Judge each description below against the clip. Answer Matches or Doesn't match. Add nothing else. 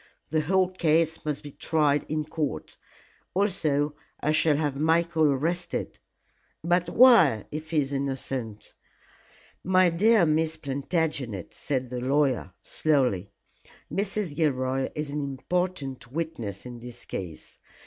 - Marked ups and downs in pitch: Doesn't match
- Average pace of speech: Doesn't match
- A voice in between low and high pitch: Matches